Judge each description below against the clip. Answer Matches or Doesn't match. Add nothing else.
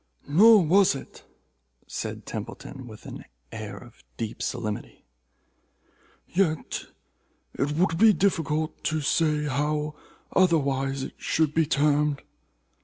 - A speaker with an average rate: Doesn't match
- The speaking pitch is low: Doesn't match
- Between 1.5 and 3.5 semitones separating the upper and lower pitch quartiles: Matches